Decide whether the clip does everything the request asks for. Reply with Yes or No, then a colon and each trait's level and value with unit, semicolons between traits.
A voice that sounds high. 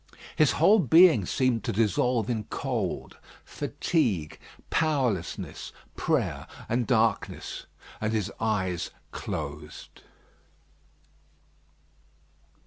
No: low, 115 Hz